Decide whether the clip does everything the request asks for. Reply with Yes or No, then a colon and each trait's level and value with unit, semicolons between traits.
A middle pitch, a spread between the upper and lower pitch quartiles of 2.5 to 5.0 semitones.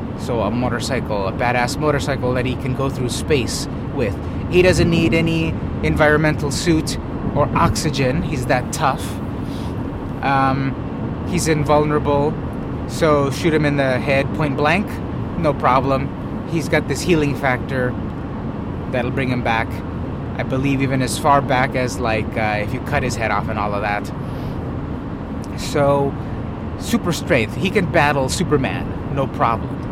No: low, 130 Hz; average, 3.9 semitones